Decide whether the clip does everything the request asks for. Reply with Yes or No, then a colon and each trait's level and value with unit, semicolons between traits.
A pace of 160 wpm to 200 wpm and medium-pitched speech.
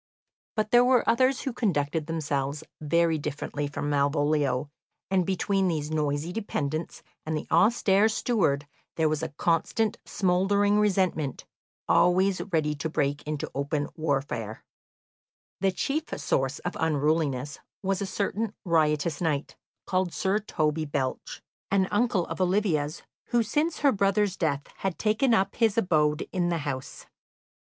No: average, 140 wpm; medium, 165 Hz